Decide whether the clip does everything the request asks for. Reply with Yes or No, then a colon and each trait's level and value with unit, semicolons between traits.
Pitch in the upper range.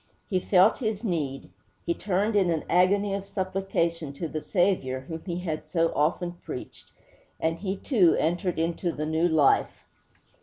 No: medium, 175 Hz